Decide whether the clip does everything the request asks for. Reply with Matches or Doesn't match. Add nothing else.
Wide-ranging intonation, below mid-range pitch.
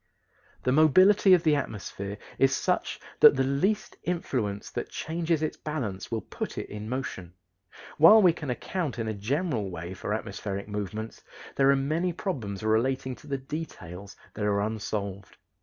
Matches